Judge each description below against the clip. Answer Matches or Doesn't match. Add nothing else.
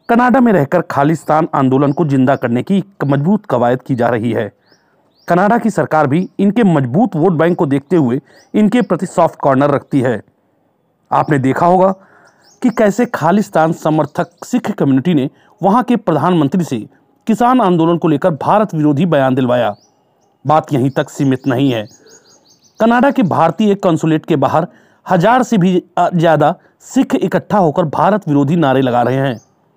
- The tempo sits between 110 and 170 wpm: Matches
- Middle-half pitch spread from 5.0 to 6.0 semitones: Matches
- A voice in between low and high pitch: Matches